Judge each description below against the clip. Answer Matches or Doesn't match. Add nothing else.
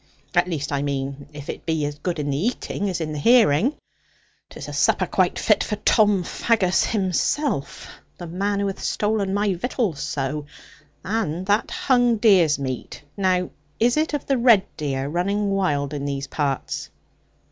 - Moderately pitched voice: Matches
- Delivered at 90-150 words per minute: Doesn't match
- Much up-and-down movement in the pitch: Matches